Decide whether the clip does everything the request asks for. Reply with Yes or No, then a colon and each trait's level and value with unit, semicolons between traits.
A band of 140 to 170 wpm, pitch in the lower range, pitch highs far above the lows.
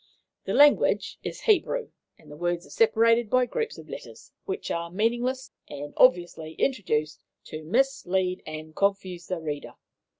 No: average, 145 wpm; high, 190 Hz; wide, 8.1 semitones